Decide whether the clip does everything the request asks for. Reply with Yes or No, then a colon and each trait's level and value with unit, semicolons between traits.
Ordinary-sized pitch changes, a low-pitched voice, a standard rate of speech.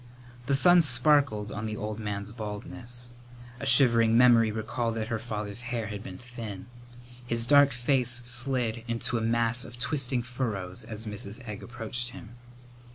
No: narrow, 2.3 semitones; low, 115 Hz; average, 160 wpm